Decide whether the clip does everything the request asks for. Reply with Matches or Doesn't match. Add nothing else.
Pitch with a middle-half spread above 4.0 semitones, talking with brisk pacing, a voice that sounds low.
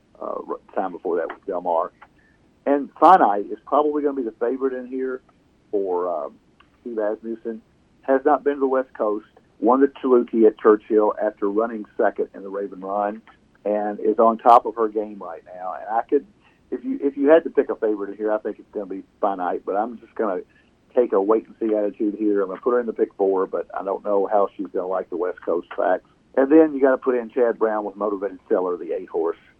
Matches